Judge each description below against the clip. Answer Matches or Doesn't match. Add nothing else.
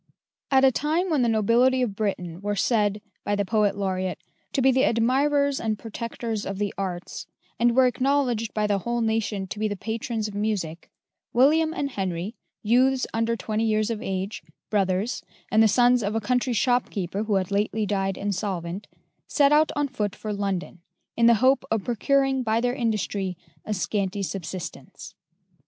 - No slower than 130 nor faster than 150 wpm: Doesn't match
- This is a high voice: Matches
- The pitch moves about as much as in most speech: Matches